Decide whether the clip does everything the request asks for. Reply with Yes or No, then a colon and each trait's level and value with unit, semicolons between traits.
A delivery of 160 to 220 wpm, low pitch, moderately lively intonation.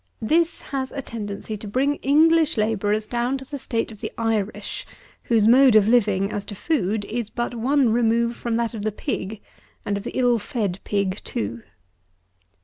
No: average, 180 wpm; high, 225 Hz; average, 3.5 semitones